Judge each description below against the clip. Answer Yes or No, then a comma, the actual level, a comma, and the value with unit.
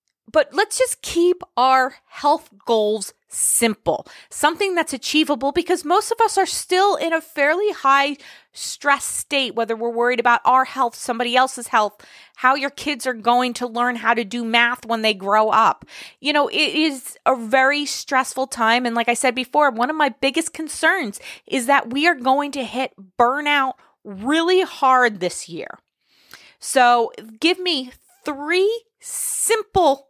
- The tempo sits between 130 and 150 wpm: No, average, 165 wpm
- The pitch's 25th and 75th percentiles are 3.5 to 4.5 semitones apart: No, average, 5.0 semitones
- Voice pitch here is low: No, very high, 270 Hz